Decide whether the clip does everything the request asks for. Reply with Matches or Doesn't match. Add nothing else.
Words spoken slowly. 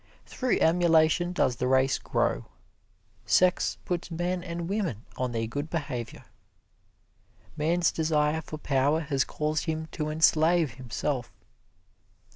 Matches